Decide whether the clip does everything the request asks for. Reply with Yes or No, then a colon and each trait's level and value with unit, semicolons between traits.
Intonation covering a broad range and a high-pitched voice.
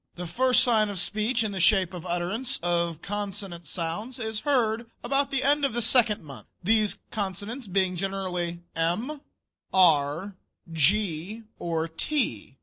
No: average, 4.8 semitones; high, 200 Hz